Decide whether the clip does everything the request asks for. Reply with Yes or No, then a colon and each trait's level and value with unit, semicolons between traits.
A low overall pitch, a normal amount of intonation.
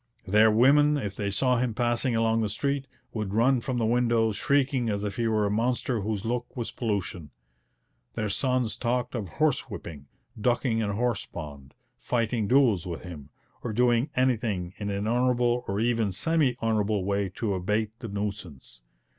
Yes: low, 115 Hz; average, 3.4 semitones